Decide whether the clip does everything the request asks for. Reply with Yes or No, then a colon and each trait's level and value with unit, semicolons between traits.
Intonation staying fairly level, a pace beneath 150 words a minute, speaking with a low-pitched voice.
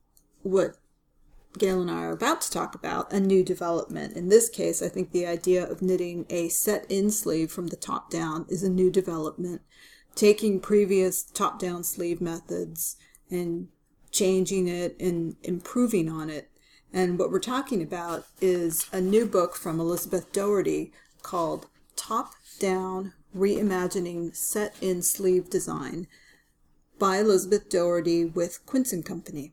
No: narrow, 2.2 semitones; average, 140 wpm; medium, 180 Hz